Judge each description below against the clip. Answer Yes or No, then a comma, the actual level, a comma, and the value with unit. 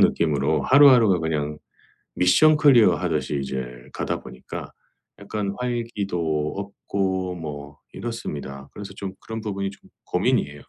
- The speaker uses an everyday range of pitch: No, wide, 6.4 semitones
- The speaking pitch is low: Yes, very low, 95 Hz